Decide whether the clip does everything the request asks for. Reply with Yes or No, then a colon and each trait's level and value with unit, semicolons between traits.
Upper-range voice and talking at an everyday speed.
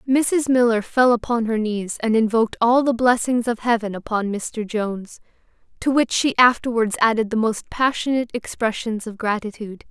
Yes: high, 230 Hz; average, 165 wpm